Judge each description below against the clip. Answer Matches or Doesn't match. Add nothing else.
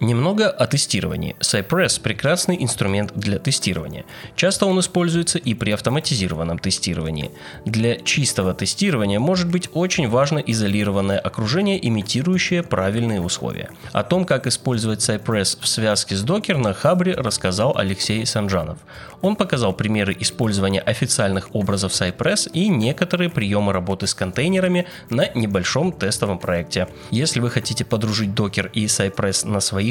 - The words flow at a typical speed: Matches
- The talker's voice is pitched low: Matches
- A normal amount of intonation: Doesn't match